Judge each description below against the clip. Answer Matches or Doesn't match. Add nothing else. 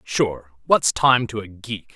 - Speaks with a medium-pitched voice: Doesn't match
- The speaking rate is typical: Matches